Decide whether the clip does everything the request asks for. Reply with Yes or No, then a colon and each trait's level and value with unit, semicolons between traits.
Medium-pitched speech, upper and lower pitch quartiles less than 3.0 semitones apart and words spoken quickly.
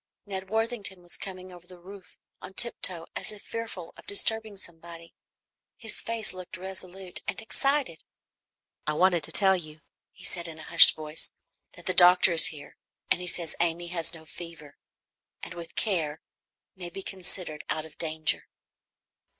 No: medium, 180 Hz; narrow, 2.6 semitones; average, 165 wpm